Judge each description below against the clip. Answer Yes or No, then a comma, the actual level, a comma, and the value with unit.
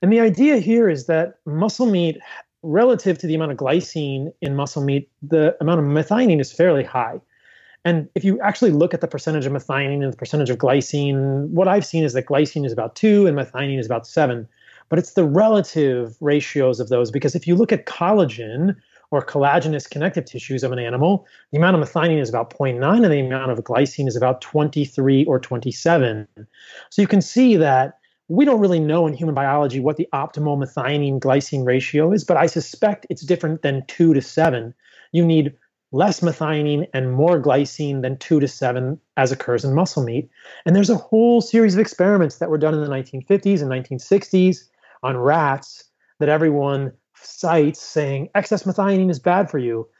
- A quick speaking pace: No, average, 195 wpm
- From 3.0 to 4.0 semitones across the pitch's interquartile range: No, average, 4.6 semitones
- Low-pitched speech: No, medium, 150 Hz